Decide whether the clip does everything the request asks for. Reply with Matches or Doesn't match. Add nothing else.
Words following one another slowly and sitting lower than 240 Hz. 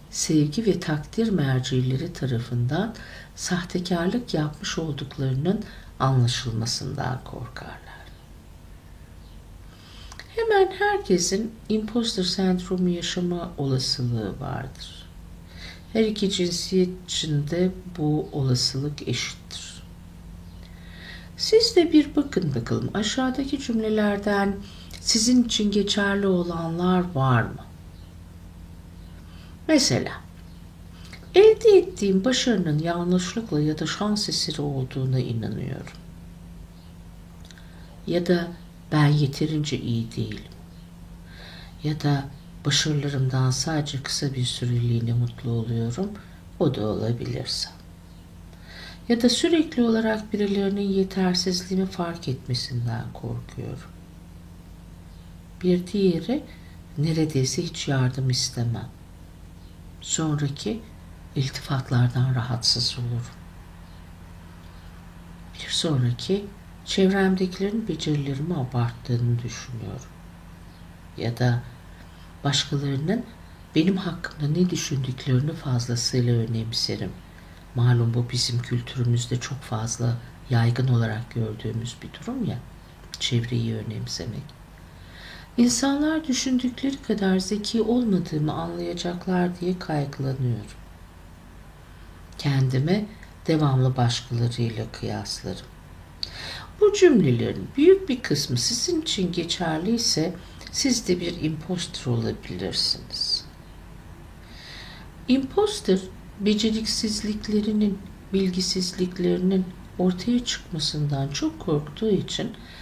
Matches